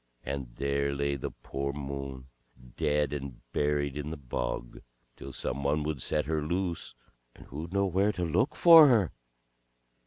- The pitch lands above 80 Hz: No, very low, 75 Hz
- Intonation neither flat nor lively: Yes, average, 3.1 semitones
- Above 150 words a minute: Yes, average, 160 wpm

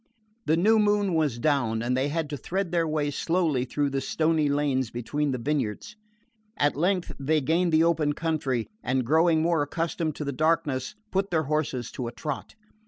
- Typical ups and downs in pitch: Yes, average, 3.6 semitones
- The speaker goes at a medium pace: Yes, average, 185 wpm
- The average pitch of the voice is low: No, medium, 150 Hz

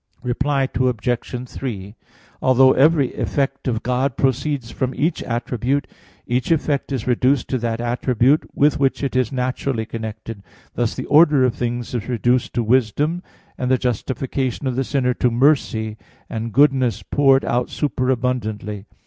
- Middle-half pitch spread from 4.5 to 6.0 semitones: No, narrow, 2.5 semitones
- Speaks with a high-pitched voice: No, low, 125 Hz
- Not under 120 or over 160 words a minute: Yes, average, 150 wpm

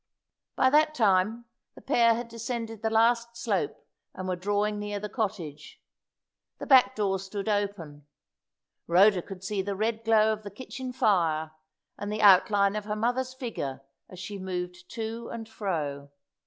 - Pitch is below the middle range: No, high, 210 Hz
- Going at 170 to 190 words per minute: No, average, 160 wpm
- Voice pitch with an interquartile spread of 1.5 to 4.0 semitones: Yes, average, 3.4 semitones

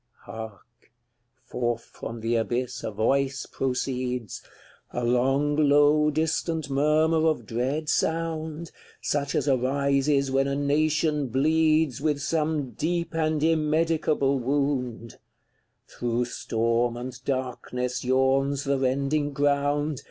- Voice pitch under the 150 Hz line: Yes, medium, 140 Hz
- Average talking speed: No, slow, 115 wpm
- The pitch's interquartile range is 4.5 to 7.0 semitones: No, average, 3.3 semitones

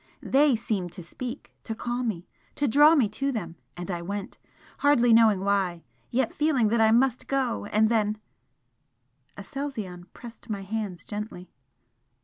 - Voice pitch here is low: No, high, 220 Hz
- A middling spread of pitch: Yes, average, 4.9 semitones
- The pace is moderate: Yes, average, 155 wpm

